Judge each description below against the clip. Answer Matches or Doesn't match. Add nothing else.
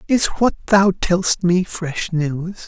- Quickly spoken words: Doesn't match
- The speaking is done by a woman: Doesn't match